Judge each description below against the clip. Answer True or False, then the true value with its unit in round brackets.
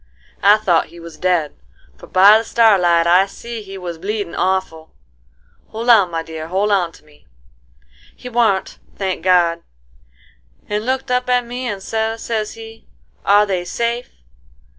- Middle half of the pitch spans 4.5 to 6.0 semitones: True (4.9 semitones)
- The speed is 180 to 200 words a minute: False (150 wpm)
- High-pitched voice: True (195 Hz)